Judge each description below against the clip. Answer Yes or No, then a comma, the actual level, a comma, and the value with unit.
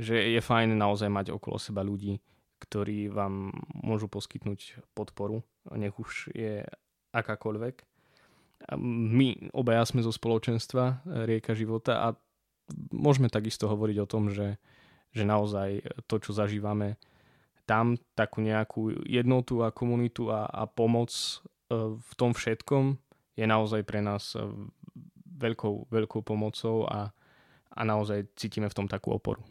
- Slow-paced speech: No, average, 130 wpm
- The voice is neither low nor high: No, low, 110 Hz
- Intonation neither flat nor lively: No, narrow, 1.9 semitones